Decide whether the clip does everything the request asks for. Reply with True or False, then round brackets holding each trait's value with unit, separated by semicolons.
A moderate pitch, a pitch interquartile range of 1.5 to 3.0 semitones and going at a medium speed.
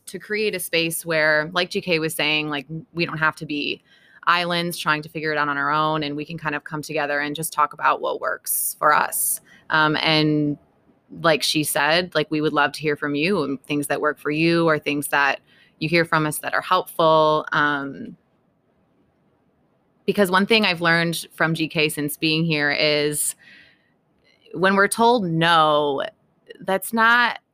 True (155 Hz; 2.5 semitones; 185 wpm)